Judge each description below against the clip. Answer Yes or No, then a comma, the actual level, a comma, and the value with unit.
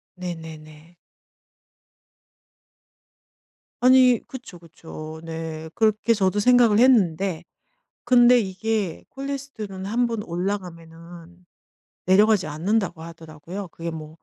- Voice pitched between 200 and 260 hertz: No, medium, 185 Hz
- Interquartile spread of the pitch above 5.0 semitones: Yes, wide, 5.4 semitones